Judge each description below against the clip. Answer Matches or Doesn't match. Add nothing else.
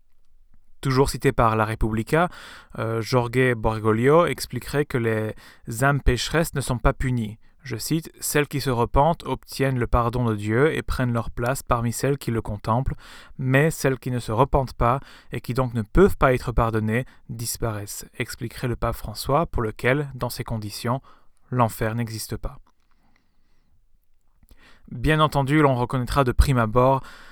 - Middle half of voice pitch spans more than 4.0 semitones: Doesn't match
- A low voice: Matches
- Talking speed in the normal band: Matches